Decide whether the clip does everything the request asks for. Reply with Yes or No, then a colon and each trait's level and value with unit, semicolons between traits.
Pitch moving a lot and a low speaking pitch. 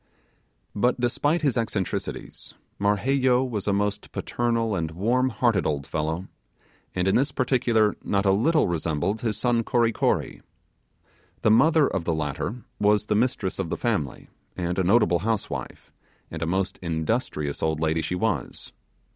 Yes: wide, 5.8 semitones; low, 105 Hz